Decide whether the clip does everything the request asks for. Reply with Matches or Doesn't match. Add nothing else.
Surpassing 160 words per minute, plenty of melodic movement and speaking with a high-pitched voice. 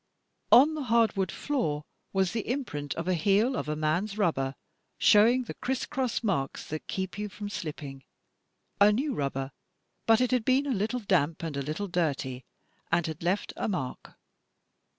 Matches